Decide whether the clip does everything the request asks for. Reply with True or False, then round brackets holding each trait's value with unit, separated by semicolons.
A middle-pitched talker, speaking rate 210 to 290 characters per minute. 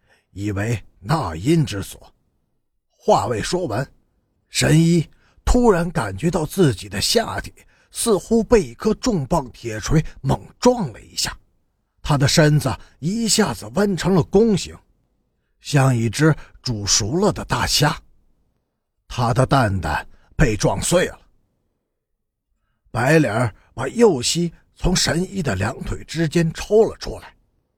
False (145 Hz; 180 characters per minute)